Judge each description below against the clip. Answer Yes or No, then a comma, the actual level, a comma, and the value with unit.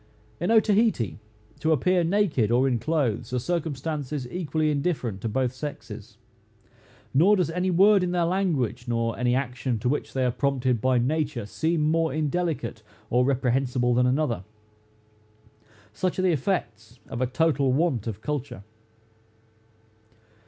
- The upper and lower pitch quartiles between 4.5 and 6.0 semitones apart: Yes, average, 5.2 semitones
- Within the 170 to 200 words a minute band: No, average, 145 wpm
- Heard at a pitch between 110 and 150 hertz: Yes, medium, 140 Hz